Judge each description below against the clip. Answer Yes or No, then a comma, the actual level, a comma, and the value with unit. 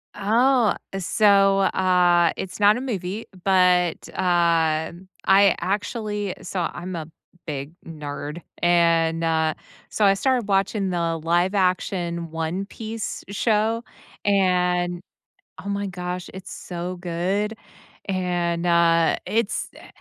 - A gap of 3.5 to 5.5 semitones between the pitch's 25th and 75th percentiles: No, average, 2.8 semitones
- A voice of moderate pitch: Yes, medium, 180 Hz